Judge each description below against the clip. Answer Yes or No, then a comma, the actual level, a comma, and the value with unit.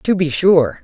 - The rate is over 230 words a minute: No, fast, 215 wpm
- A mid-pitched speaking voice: Yes, medium, 170 Hz